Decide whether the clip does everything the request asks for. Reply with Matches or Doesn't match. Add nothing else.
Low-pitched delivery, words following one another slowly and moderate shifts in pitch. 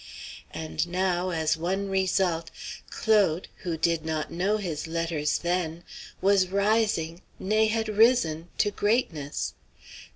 Doesn't match